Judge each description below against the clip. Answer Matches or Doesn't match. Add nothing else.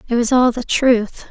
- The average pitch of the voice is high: Matches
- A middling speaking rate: Doesn't match